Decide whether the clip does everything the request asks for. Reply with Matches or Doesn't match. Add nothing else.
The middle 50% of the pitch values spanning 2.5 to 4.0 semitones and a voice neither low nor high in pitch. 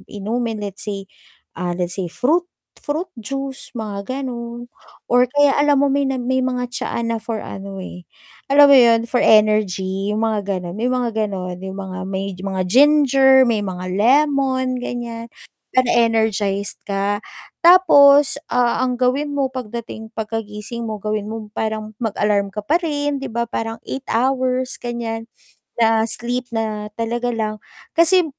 Doesn't match